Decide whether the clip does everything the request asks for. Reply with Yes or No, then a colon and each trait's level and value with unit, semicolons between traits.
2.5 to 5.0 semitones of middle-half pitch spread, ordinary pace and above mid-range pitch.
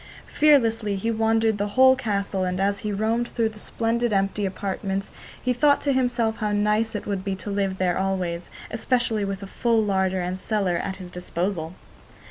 Yes: average, 2.9 semitones; average, 185 wpm; high, 205 Hz